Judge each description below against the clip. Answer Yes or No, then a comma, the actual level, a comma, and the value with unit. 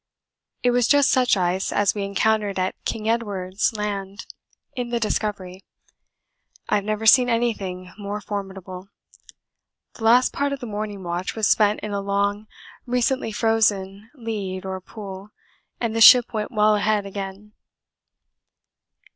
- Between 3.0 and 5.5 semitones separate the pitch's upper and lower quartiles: No, narrow, 2.5 semitones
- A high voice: Yes, high, 210 Hz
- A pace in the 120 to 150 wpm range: Yes, average, 145 wpm